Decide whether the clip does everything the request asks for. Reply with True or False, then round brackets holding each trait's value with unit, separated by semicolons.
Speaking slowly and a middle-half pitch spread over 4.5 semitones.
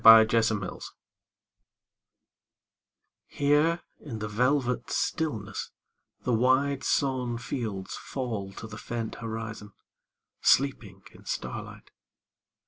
False (95 wpm; 3.5 semitones)